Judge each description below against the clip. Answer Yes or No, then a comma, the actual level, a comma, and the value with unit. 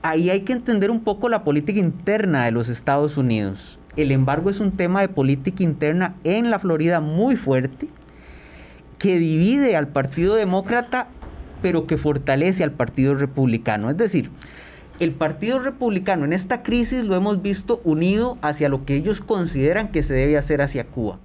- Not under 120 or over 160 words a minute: No, average, 170 wpm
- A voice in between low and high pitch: Yes, medium, 165 Hz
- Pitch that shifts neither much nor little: No, wide, 6.6 semitones